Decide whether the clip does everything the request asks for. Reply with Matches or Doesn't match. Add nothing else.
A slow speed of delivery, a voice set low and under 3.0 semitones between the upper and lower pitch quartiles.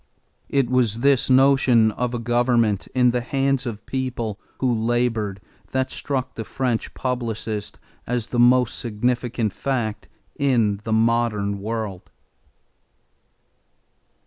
Matches